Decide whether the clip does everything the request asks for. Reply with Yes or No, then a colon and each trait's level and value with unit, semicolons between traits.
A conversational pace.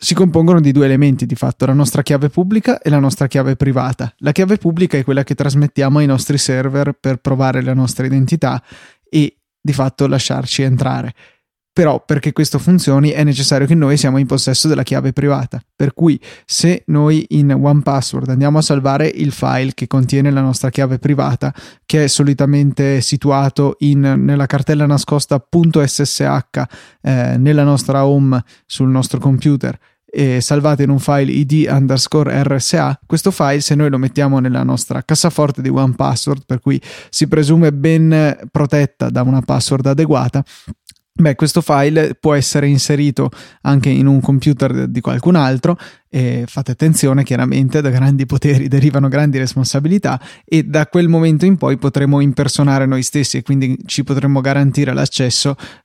Yes: average, 160 wpm